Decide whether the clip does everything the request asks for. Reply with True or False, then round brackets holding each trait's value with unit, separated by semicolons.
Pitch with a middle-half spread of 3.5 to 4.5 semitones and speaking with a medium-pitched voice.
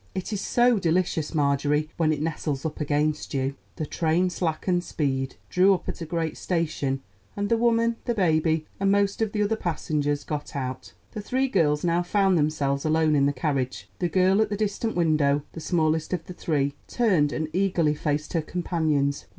True (4.2 semitones; 160 Hz)